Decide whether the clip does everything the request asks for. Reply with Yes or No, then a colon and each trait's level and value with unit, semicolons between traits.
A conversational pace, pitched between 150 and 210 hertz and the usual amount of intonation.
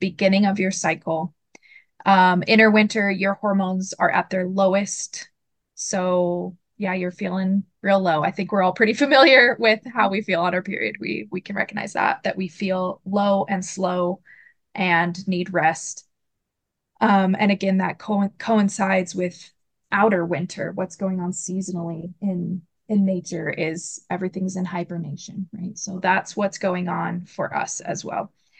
No: average, 160 wpm; high, 190 Hz; narrow, 1.9 semitones